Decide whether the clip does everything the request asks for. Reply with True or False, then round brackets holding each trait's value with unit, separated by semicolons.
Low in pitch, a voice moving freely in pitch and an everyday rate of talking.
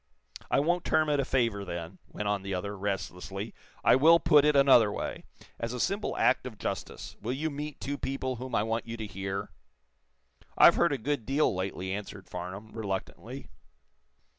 True (115 Hz; 6.0 semitones; 185 wpm)